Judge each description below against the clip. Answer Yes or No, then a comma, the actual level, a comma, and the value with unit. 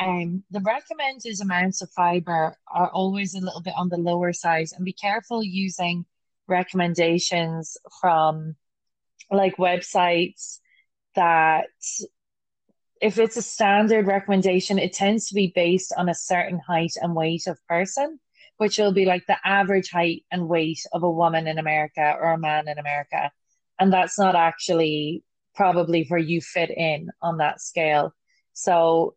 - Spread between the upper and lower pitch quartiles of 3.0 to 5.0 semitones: No, narrow, 2.6 semitones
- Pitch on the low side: No, medium, 175 Hz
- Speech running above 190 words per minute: No, average, 150 wpm